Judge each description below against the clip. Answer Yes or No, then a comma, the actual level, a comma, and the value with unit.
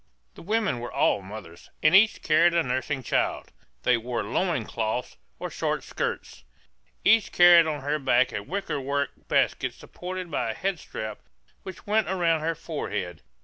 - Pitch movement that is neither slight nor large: No, wide, 6.5 semitones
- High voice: No, medium, 150 Hz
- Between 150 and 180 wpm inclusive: Yes, average, 160 wpm